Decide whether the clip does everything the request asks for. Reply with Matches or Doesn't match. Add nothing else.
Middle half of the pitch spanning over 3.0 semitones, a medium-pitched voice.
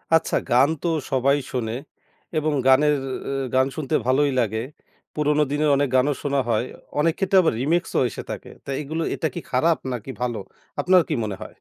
Matches